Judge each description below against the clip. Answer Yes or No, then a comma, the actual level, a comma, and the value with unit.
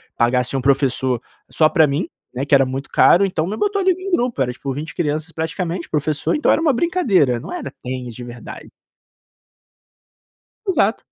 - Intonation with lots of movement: Yes, wide, 7.4 semitones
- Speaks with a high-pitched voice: No, medium, 155 Hz